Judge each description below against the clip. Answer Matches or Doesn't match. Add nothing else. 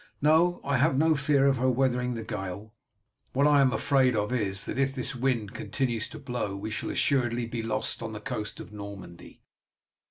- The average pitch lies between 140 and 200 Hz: Doesn't match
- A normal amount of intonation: Matches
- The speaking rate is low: Doesn't match